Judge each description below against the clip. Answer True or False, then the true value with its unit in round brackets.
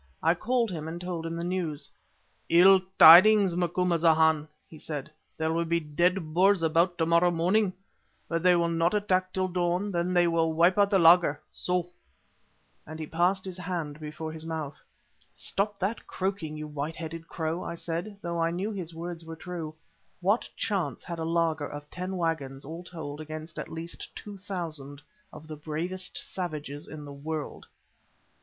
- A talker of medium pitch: True (170 Hz)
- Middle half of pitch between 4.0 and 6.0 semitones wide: False (2.4 semitones)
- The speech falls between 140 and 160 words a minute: False (175 wpm)